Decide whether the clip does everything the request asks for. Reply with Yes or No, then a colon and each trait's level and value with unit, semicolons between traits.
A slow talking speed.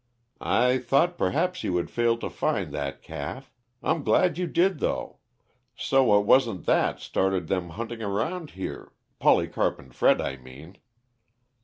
No: average, 150 wpm